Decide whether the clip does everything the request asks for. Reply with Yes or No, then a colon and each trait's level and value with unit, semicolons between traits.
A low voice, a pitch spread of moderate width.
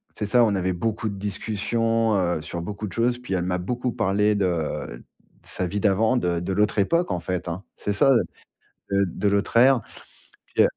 Yes: low, 100 Hz; average, 3.8 semitones